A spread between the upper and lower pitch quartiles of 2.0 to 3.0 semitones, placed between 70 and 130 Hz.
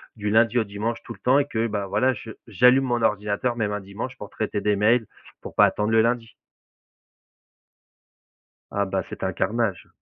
Yes: narrow, 2.5 semitones; low, 110 Hz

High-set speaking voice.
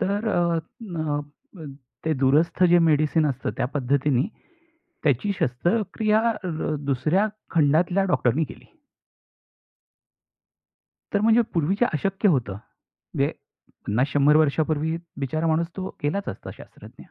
No: medium, 160 Hz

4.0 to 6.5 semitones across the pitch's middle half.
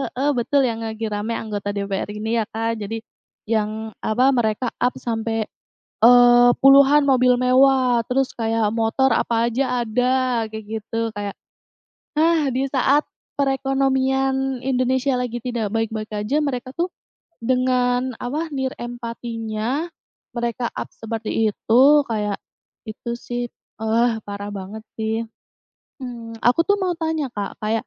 No: average, 2.9 semitones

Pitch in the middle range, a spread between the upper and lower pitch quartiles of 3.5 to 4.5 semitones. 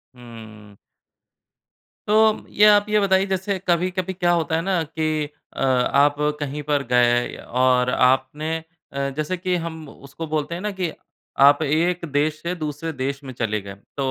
No: medium, 155 Hz; average, 5.0 semitones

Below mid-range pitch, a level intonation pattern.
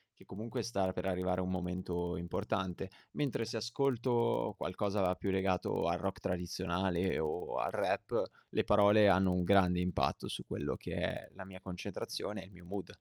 Yes: very low, 95 Hz; narrow, 2.2 semitones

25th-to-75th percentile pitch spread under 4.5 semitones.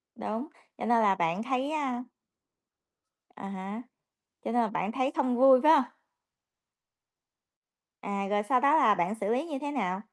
No: average, 5.1 semitones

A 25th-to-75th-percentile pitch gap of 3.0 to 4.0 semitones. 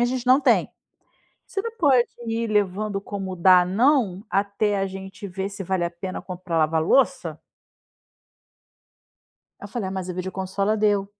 No: narrow, 2.5 semitones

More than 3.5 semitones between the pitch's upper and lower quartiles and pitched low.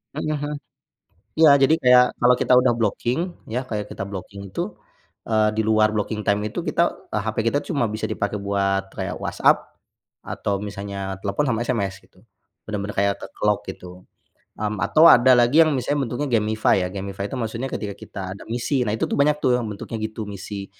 Yes: average, 4.0 semitones; low, 110 Hz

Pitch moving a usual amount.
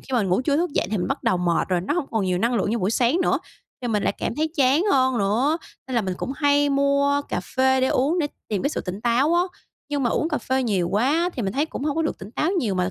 No: wide, 5.7 semitones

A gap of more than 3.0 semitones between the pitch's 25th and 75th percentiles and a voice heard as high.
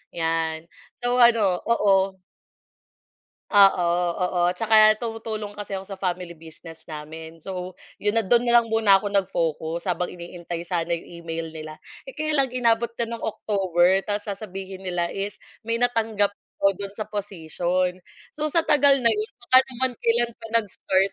Yes: average, 4.3 semitones; high, 195 Hz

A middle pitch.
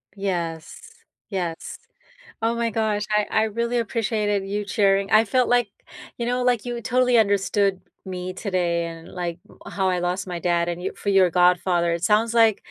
No: high, 200 Hz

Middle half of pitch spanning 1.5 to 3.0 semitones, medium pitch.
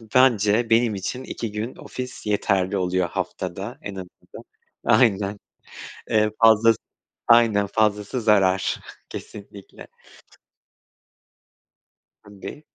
No: narrow, 2.6 semitones; low, 105 Hz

